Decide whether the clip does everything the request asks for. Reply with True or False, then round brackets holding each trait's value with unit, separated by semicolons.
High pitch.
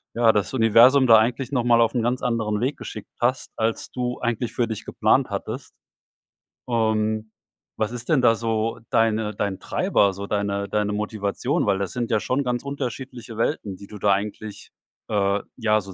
False (110 Hz)